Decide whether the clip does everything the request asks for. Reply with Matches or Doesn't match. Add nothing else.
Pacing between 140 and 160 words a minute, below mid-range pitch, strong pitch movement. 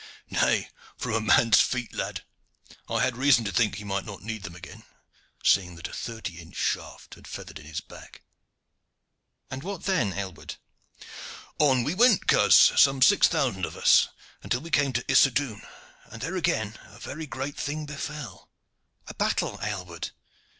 Doesn't match